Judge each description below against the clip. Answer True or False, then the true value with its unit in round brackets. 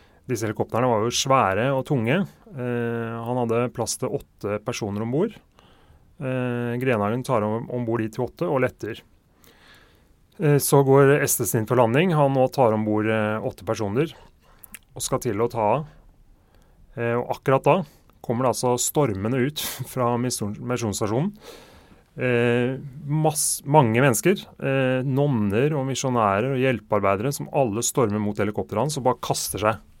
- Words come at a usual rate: True (150 wpm)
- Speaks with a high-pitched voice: False (125 Hz)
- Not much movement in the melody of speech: False (3.9 semitones)